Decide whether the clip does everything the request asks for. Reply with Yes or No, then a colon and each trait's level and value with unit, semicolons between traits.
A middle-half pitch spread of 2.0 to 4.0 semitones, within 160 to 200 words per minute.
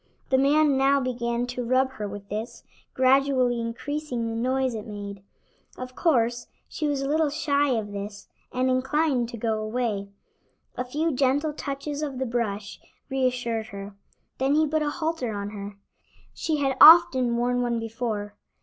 Yes: average, 3.6 semitones; average, 165 wpm